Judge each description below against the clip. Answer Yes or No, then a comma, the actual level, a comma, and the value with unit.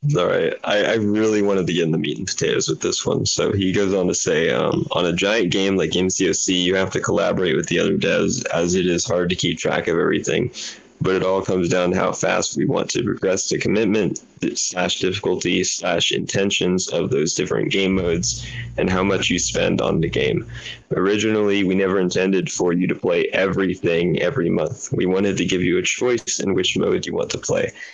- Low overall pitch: Yes, very low, 95 Hz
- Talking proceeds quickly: Yes, fast, 220 wpm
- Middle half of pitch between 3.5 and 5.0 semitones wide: No, average, 2.7 semitones